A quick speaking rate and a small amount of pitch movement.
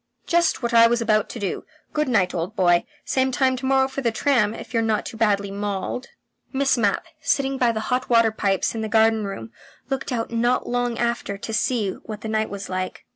No: fast, 220 wpm; average, 3.4 semitones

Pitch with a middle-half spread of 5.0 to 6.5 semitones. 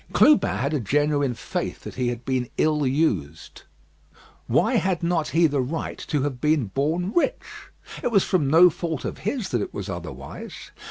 Yes: average, 5.3 semitones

